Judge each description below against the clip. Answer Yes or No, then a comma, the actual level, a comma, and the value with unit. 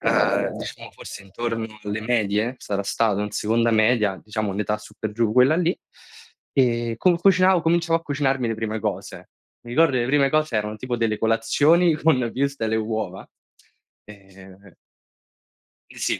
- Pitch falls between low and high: No, low, 115 Hz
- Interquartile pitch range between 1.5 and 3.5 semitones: No, average, 4.4 semitones